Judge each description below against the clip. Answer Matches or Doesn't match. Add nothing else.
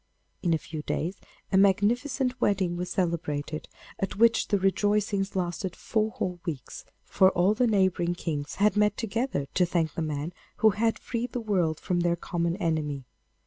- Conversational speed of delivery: Matches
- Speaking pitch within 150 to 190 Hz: Matches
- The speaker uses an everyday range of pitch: Matches